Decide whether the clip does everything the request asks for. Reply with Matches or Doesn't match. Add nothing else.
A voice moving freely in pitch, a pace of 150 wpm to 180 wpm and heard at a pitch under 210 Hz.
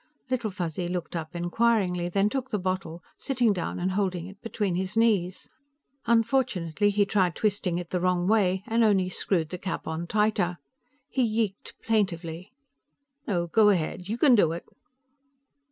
Doesn't match